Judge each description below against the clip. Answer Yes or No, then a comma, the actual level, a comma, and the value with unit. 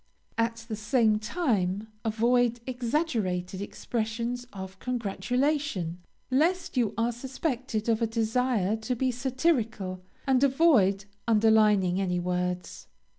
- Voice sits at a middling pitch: No, high, 230 Hz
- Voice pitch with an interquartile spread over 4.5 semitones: No, average, 4.1 semitones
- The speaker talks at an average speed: No, slow, 110 wpm